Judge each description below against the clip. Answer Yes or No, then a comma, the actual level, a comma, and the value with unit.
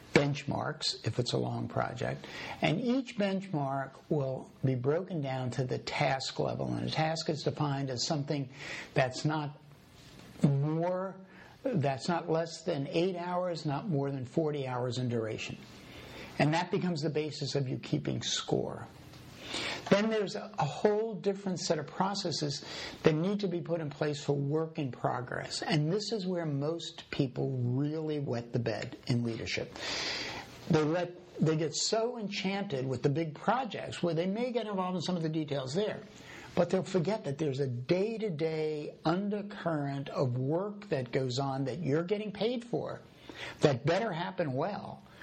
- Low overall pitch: No, medium, 160 Hz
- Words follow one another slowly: No, average, 165 wpm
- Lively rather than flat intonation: No, average, 4.5 semitones